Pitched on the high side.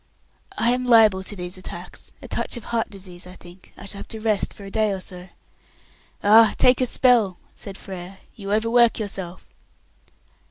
Yes: high, 200 Hz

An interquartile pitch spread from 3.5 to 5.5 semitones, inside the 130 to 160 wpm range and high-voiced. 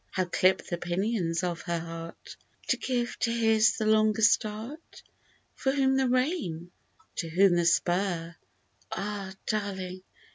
Yes: average, 4.9 semitones; average, 145 wpm; high, 200 Hz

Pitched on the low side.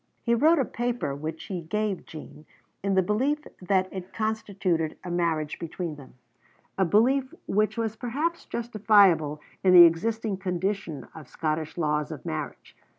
No: high, 190 Hz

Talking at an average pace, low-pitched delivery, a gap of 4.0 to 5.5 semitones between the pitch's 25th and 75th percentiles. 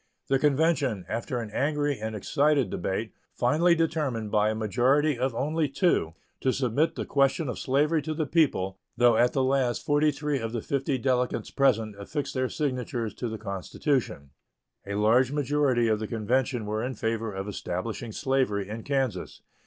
Yes: average, 170 wpm; low, 130 Hz; average, 4.6 semitones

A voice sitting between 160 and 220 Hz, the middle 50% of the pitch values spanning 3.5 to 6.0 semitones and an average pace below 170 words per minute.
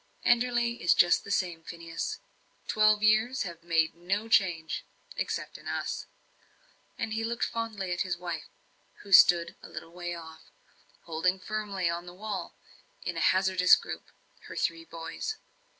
Yes: medium, 185 Hz; average, 4.1 semitones; average, 150 wpm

